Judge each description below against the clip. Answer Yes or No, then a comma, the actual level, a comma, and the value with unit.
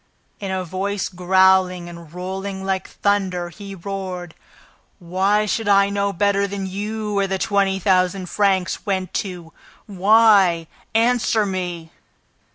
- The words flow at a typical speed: No, slow, 130 wpm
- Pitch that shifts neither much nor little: No, narrow, 1.8 semitones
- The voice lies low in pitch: No, high, 190 Hz